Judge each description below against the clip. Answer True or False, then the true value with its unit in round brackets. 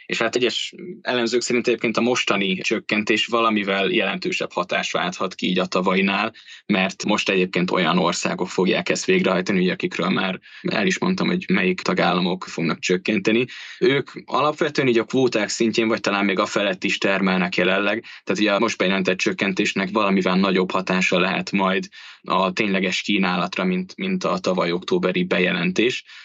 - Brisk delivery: True (160 wpm)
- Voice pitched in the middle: False (110 Hz)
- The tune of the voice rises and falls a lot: True (7.9 semitones)